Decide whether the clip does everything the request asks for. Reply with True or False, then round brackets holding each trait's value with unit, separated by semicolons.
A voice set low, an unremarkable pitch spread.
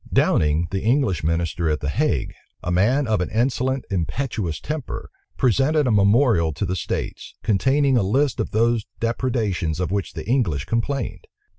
False (110 Hz; 6.9 semitones)